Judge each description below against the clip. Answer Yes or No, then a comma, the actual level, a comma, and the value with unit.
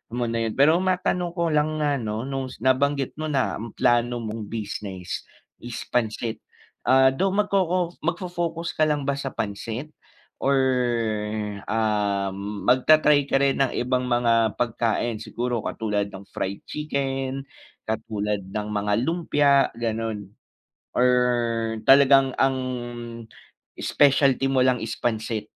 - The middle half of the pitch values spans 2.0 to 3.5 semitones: No, average, 4.3 semitones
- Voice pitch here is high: No, low, 125 Hz